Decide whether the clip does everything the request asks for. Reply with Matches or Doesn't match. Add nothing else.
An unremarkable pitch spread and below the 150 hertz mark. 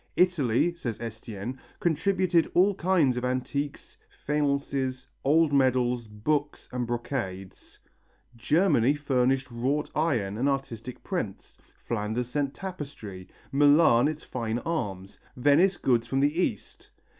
Matches